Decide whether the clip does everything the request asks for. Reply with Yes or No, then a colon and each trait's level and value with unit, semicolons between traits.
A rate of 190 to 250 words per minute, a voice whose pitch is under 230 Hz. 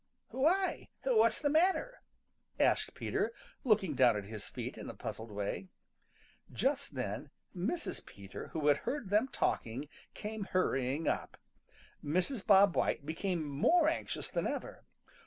No: average, 140 wpm; medium, 185 Hz